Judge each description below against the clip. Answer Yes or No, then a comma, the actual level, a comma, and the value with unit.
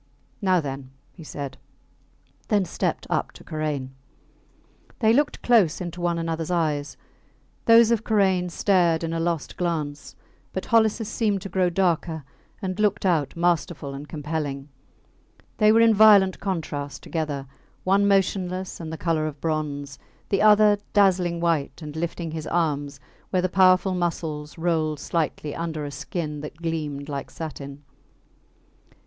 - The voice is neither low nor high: Yes, medium, 170 Hz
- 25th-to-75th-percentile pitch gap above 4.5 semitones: No, average, 3.9 semitones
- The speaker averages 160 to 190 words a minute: No, average, 145 wpm